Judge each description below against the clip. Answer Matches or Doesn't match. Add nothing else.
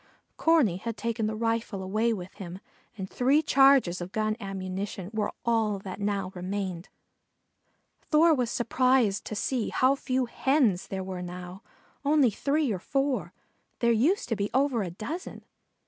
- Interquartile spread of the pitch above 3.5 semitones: Matches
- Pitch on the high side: Matches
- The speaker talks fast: Doesn't match